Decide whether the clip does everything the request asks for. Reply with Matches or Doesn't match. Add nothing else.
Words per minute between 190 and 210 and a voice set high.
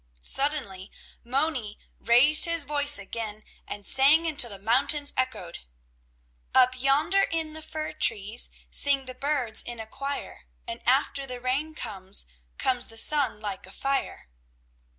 Doesn't match